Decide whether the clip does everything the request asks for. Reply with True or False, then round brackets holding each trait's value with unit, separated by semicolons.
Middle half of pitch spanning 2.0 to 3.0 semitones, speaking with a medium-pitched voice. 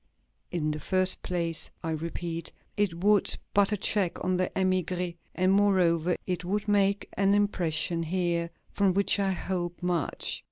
True (2.6 semitones; 180 Hz)